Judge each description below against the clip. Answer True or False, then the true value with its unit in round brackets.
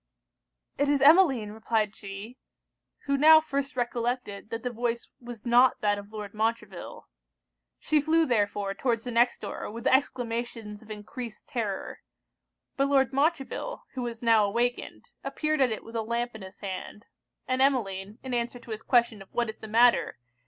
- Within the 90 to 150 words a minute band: False (170 wpm)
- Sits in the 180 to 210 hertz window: False (235 Hz)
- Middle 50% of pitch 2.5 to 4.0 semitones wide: True (3.4 semitones)